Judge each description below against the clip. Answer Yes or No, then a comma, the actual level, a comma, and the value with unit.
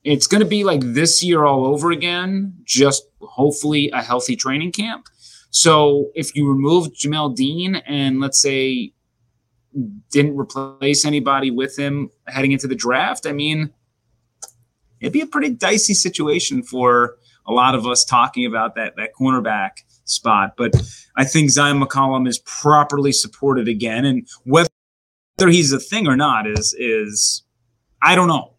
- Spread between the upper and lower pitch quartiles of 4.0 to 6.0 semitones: No, average, 3.6 semitones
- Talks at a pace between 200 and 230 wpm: No, average, 155 wpm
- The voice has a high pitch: No, medium, 140 Hz